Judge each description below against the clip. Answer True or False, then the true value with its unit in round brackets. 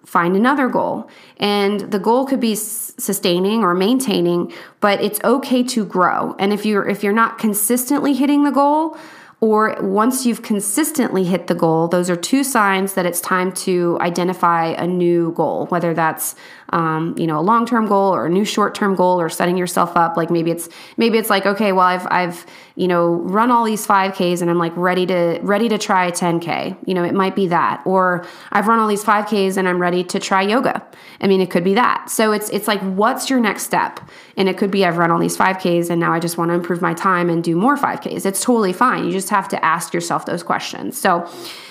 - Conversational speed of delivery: False (225 wpm)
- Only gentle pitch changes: False (3.8 semitones)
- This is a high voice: True (195 Hz)